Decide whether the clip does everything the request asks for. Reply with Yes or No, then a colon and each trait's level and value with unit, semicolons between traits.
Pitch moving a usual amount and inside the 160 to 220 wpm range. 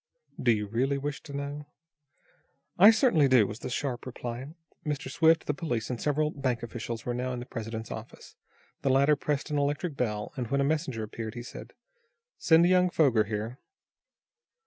Yes: average, 3.9 semitones; average, 180 wpm